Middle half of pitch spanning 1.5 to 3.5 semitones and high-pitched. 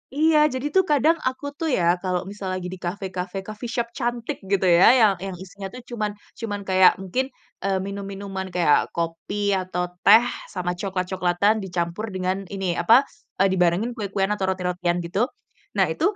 Yes: average, 2.9 semitones; high, 195 Hz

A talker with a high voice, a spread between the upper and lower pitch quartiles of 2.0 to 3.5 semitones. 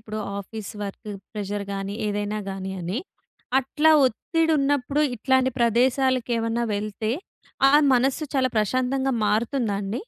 No: high, 230 Hz; average, 4.1 semitones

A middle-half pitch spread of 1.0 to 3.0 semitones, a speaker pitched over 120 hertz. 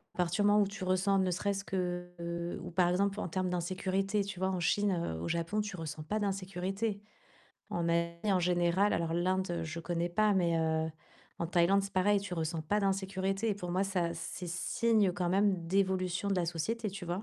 Yes: narrow, 2.4 semitones; medium, 185 Hz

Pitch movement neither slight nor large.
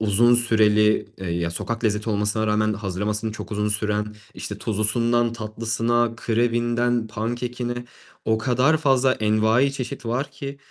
No: narrow, 2.2 semitones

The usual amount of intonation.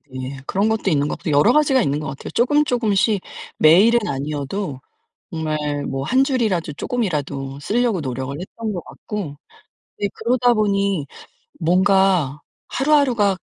No: wide, 7.9 semitones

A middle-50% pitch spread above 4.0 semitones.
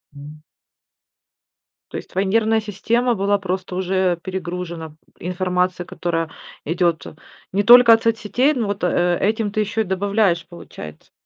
No: average, 3.6 semitones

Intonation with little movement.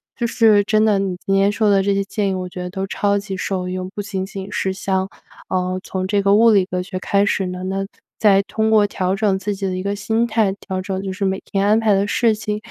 Yes: narrow, 1.7 semitones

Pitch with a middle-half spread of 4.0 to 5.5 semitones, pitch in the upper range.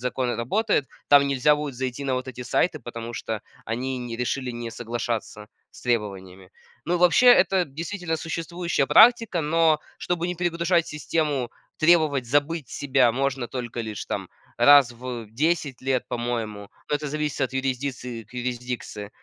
No: average, 4.8 semitones; low, 130 Hz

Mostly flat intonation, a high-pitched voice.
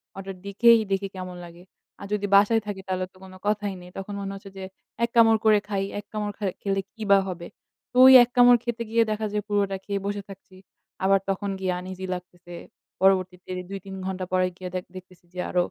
Yes: narrow, 2.0 semitones; high, 195 Hz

